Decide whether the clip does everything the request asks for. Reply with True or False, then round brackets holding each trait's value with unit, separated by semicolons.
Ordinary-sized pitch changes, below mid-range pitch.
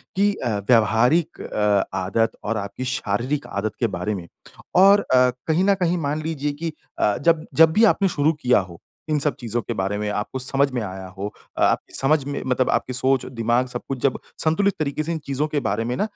False (6.0 semitones; 130 Hz)